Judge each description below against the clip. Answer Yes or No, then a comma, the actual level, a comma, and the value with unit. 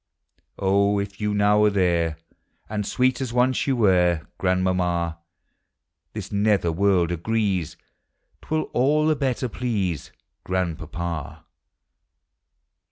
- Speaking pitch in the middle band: No, low, 100 Hz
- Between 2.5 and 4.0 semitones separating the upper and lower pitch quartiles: No, average, 4.5 semitones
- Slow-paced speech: Yes, slow, 110 wpm